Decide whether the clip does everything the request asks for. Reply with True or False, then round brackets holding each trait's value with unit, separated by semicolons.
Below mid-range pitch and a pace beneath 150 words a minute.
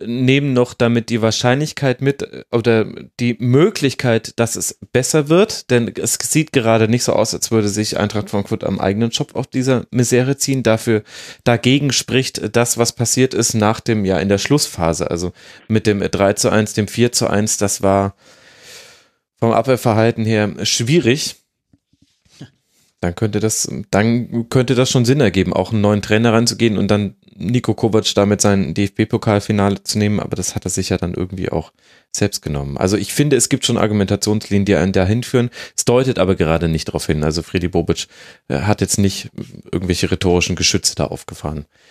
False (110 Hz; 175 wpm)